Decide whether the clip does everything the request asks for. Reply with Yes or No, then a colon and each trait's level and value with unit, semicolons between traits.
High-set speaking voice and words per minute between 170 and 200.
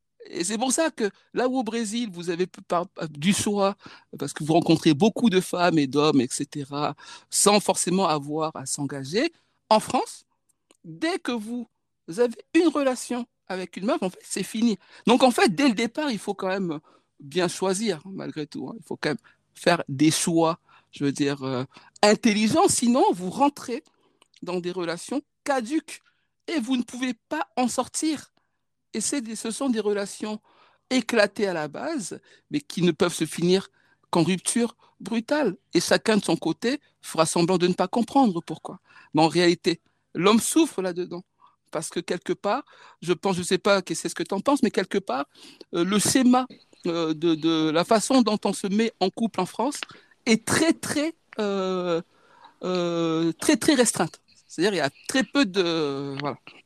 Yes: high, 200 Hz; average, 185 wpm